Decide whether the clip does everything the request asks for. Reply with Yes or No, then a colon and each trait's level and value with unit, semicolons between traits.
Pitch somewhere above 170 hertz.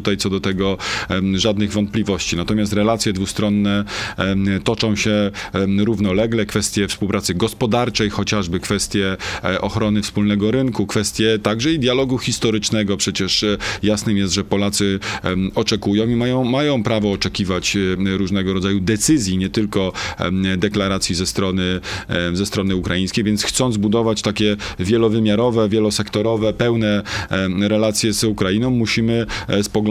No: low, 105 Hz